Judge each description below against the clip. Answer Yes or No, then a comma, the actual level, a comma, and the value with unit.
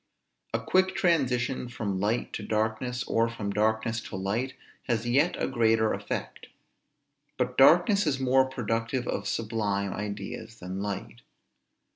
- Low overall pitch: Yes, low, 115 Hz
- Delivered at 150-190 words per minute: No, slow, 135 wpm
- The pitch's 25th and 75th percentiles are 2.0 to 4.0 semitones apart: Yes, average, 3.6 semitones